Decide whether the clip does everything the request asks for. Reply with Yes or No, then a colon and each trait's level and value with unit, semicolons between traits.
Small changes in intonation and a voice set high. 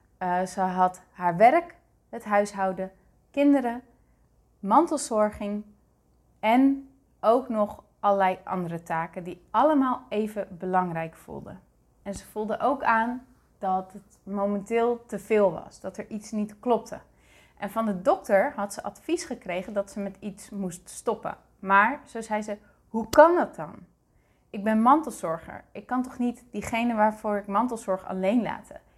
No: average, 3.4 semitones; high, 210 Hz